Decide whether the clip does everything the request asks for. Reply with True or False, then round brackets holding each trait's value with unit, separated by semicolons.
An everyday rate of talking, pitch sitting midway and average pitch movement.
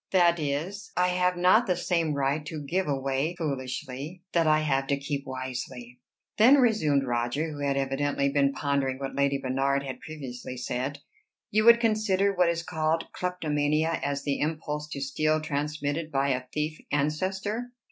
True (165 wpm; 150 Hz; 3.8 semitones)